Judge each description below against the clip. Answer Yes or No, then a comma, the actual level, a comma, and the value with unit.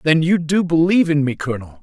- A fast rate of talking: Yes, fast, 230 wpm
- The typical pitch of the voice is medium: Yes, medium, 155 Hz